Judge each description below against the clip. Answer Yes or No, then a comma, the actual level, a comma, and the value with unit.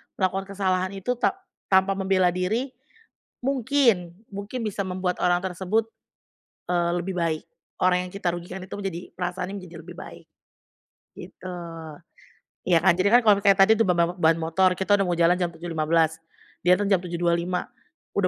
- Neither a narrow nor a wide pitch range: No, narrow, 2.2 semitones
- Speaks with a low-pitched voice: No, medium, 185 Hz